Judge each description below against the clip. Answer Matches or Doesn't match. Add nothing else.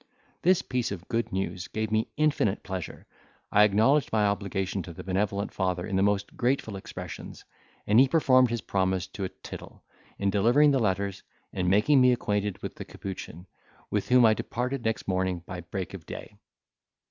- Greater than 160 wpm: Matches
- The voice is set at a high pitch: Doesn't match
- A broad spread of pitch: Doesn't match